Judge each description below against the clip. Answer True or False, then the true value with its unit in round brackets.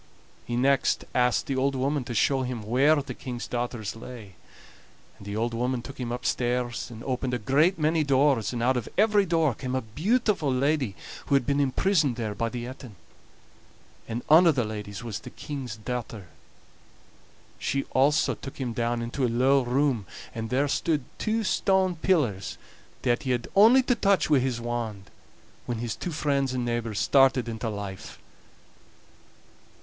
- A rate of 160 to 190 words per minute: True (175 wpm)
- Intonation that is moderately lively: True (3.4 semitones)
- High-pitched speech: False (125 Hz)